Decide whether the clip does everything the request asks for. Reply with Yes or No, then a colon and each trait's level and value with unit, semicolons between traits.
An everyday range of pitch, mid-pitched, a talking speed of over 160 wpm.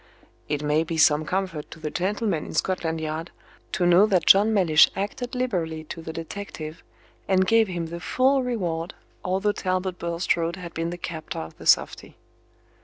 Yes: average, 3.2 semitones; medium, 175 Hz; average, 175 wpm